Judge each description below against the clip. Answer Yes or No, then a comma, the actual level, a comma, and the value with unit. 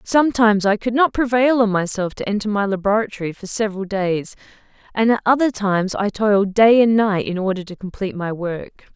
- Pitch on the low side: No, high, 210 Hz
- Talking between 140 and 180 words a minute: No, average, 195 wpm